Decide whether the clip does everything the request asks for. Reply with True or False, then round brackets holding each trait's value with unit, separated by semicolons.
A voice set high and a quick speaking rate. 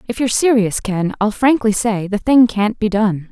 True (215 Hz; 215 wpm)